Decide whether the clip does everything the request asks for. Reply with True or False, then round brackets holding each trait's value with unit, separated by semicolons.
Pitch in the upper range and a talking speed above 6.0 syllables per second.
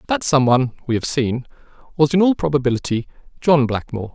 False (140 Hz; 6.3 syllables/s)